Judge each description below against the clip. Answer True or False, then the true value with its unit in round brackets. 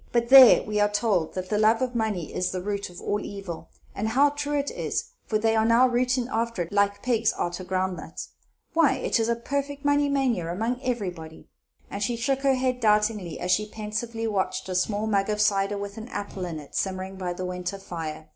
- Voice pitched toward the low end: False (210 Hz)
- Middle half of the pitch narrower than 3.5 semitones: False (4.4 semitones)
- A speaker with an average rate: False (220 wpm)